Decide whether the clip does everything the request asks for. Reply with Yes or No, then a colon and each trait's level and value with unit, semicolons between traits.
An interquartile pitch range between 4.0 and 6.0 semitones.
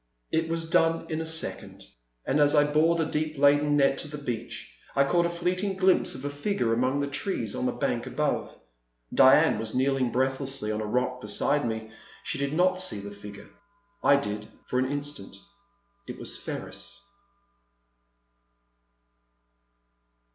Yes: average, 4.3 semitones